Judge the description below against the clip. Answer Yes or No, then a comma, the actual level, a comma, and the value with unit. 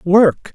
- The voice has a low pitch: No, high, 190 Hz